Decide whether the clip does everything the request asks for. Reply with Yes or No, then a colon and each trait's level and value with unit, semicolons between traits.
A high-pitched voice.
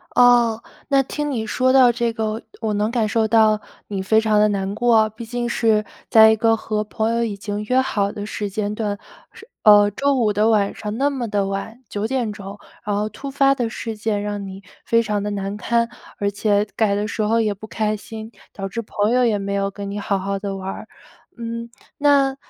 Yes: high, 215 Hz